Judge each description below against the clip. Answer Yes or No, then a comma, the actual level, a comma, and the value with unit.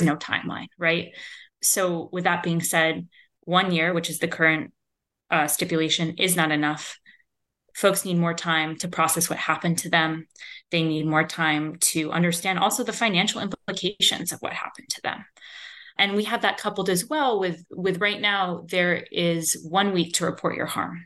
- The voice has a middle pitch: Yes, medium, 175 Hz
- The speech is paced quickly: No, average, 180 wpm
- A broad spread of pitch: No, average, 3.3 semitones